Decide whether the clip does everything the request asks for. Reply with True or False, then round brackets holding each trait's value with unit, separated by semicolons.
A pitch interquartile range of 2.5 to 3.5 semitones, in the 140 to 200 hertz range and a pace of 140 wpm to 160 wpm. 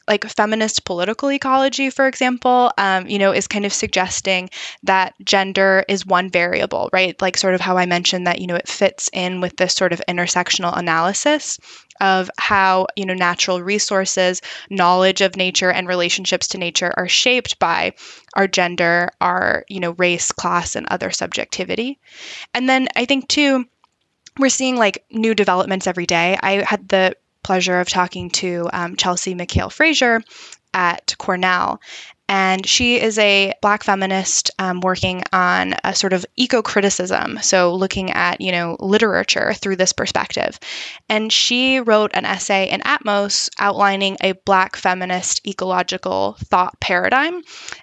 True (2.9 semitones; 190 Hz; 155 wpm)